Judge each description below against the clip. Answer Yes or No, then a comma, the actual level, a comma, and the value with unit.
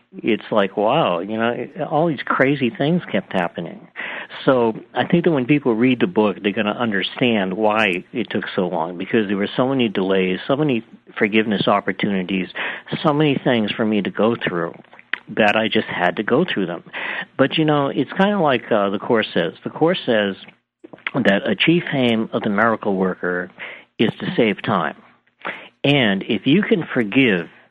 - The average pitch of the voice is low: Yes, low, 115 Hz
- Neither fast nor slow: Yes, average, 185 wpm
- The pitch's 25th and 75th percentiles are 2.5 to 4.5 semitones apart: No, wide, 5.4 semitones